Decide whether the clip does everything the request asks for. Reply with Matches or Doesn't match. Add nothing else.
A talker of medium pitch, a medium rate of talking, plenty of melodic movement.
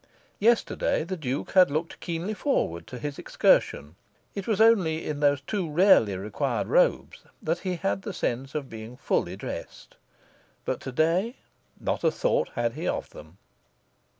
Matches